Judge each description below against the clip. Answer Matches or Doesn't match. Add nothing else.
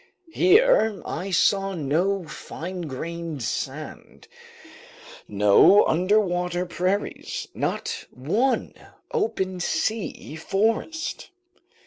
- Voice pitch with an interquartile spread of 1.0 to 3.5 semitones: Doesn't match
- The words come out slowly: Matches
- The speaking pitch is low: Doesn't match